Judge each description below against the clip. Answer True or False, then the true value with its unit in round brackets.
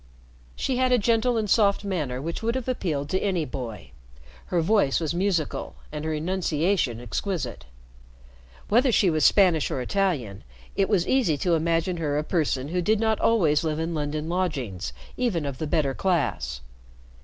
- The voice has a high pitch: False (165 Hz)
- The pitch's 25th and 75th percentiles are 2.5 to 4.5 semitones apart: False (5.3 semitones)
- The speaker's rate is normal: True (170 wpm)